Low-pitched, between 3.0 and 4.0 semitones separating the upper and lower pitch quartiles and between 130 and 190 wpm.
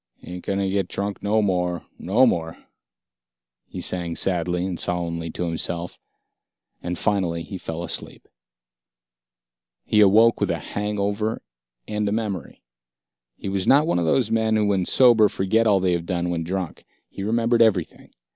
Yes: very low, 95 Hz; average, 3.4 semitones; average, 155 wpm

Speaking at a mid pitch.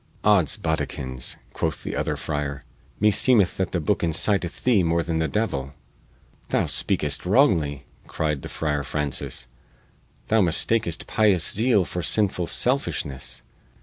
No: very low, 85 Hz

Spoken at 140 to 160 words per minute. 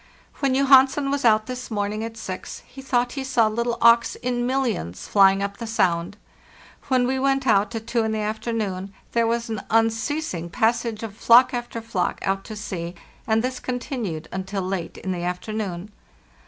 No: average, 180 wpm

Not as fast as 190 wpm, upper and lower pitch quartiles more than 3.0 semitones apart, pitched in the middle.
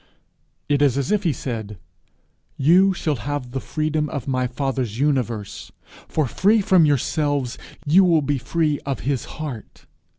Yes: average, 155 wpm; average, 3.5 semitones; medium, 145 Hz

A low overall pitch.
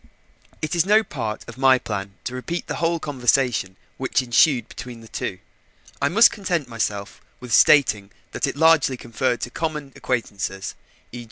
Yes: low, 130 Hz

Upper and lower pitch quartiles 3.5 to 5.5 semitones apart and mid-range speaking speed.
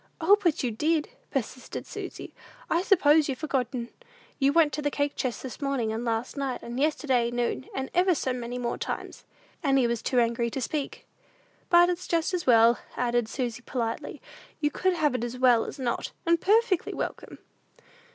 Yes: average, 4.6 semitones; average, 180 wpm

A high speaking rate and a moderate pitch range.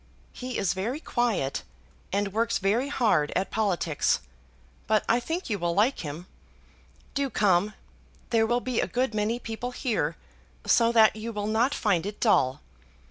No: average, 160 wpm; average, 3.7 semitones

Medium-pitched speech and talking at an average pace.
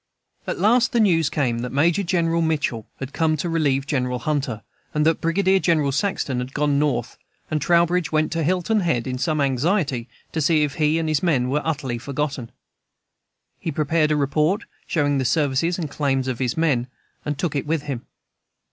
Yes: medium, 150 Hz; average, 190 wpm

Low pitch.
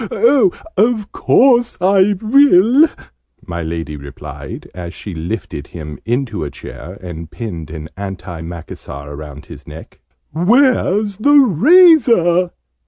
Yes: low, 115 Hz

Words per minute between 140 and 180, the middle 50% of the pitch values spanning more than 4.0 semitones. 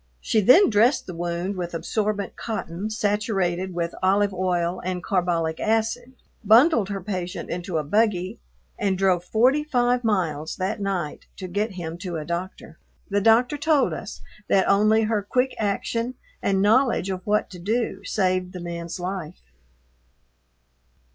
No: average, 150 wpm; average, 3.6 semitones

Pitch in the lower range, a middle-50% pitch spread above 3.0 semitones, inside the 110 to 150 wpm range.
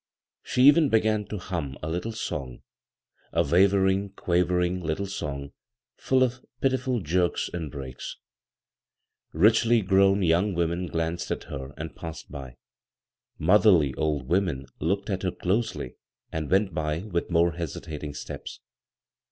Yes: very low, 90 Hz; average, 4.3 semitones; slow, 135 wpm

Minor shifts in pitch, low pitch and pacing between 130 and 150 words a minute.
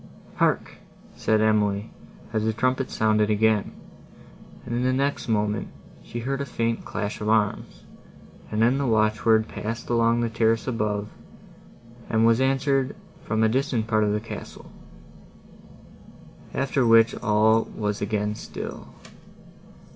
Yes: narrow, 1.9 semitones; low, 110 Hz; slow, 135 wpm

